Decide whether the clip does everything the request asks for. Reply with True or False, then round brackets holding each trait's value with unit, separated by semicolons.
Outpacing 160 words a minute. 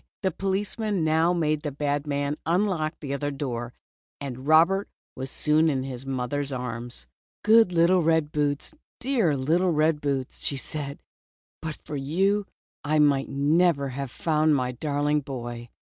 False (155 wpm)